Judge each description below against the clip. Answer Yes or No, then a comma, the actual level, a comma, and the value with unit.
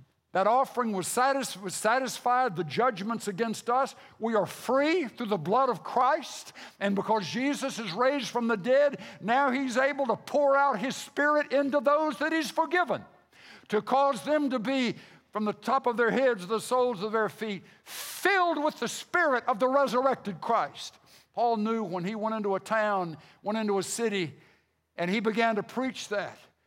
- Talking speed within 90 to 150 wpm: No, average, 180 wpm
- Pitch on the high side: Yes, high, 240 Hz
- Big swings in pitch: No, average, 4.3 semitones